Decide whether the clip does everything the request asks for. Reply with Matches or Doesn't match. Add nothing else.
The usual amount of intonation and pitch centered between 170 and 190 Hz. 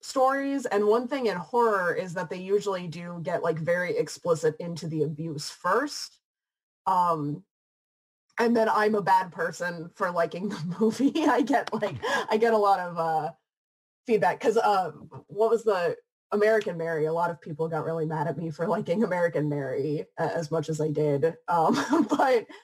Doesn't match